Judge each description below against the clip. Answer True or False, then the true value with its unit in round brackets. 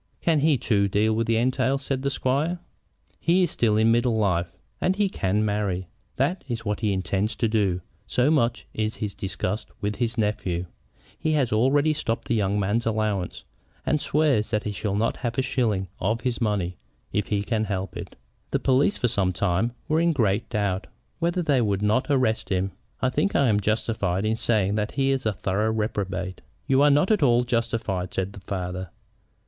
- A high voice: False (110 Hz)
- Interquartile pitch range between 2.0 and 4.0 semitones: False (4.5 semitones)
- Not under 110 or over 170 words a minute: False (195 wpm)